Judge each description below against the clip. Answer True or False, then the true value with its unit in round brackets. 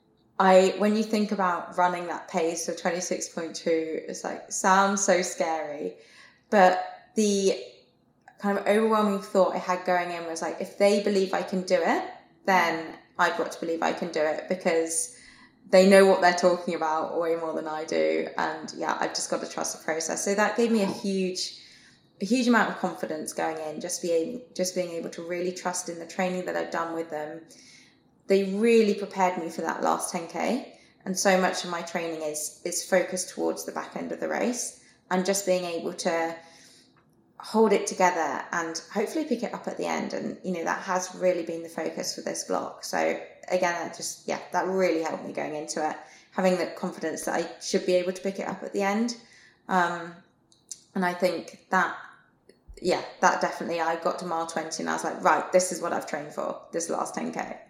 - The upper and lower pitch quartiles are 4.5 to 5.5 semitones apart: False (2.6 semitones)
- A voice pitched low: False (180 Hz)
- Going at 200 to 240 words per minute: True (205 wpm)